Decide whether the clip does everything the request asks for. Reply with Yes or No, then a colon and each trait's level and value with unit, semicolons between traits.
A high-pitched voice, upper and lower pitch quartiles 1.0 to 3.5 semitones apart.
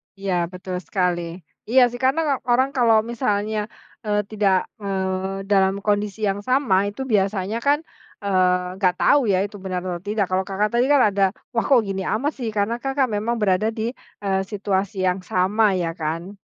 Yes: high, 200 Hz; average, 2.9 semitones